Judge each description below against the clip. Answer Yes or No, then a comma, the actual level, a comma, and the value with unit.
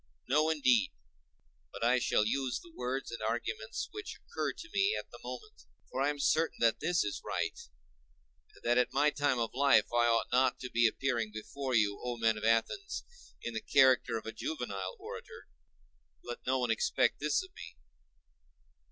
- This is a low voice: Yes, low, 125 Hz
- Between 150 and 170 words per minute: No, average, 185 wpm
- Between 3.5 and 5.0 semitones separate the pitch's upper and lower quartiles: Yes, average, 4.1 semitones